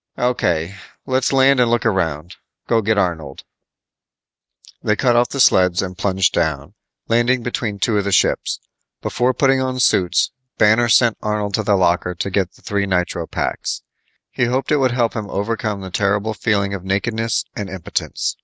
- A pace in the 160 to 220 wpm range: Yes, average, 170 wpm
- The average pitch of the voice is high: No, low, 105 Hz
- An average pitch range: Yes, average, 4.2 semitones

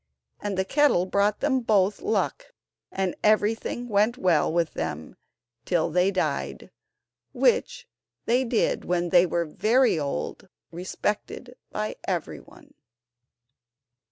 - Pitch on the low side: No, high, 200 Hz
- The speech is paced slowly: Yes, slow, 115 wpm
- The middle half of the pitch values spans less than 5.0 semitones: No, average, 5.3 semitones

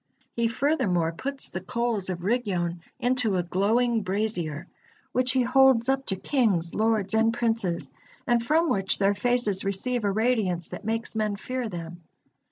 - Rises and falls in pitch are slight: No, average, 4.6 semitones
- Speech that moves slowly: No, average, 160 wpm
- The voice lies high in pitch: Yes, high, 220 Hz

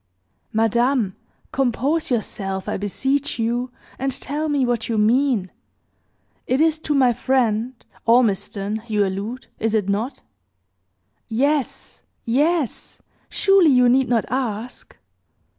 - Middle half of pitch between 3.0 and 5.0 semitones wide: Yes, average, 3.8 semitones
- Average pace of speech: No, slow, 115 wpm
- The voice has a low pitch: No, high, 245 Hz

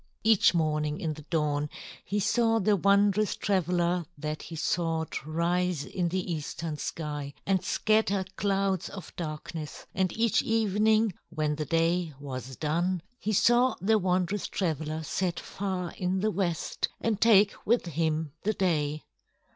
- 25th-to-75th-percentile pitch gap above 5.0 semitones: No, average, 4.2 semitones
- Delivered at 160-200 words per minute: No, average, 145 wpm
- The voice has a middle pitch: Yes, medium, 180 Hz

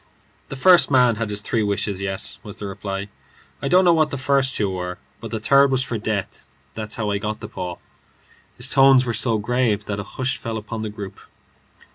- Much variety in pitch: No, average, 4.1 semitones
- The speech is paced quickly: Yes, fast, 215 wpm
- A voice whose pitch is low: Yes, low, 110 Hz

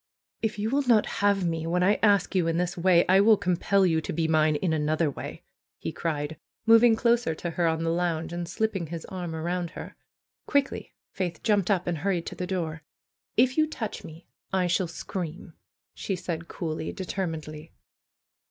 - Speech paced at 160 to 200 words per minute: Yes, average, 190 wpm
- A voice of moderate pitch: Yes, medium, 175 Hz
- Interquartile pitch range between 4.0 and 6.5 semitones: No, average, 3.5 semitones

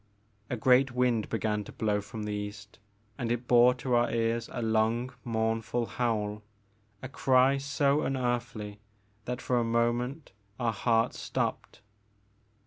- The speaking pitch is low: Yes, low, 120 Hz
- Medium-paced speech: Yes, average, 145 wpm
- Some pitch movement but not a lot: No, narrow, 2.2 semitones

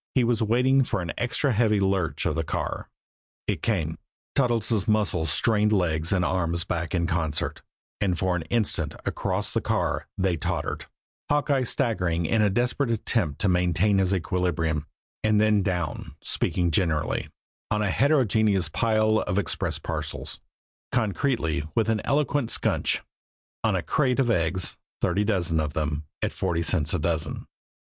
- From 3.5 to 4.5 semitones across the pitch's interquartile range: No, average, 5.1 semitones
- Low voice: Yes, very low, 95 Hz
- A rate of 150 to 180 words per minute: Yes, average, 155 wpm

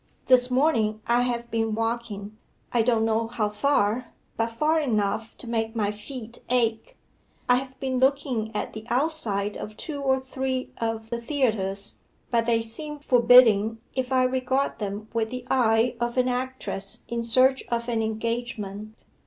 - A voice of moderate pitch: No, high, 235 Hz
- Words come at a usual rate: Yes, average, 160 wpm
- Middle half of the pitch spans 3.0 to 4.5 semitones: No, narrow, 2.6 semitones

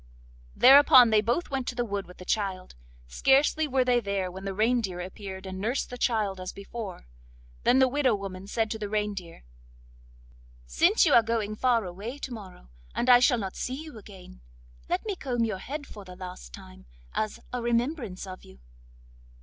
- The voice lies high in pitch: Yes, high, 215 Hz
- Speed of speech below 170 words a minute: No, average, 190 wpm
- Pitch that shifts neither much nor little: Yes, average, 4.7 semitones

